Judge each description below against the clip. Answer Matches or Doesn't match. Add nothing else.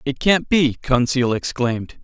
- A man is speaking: Matches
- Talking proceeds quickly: Doesn't match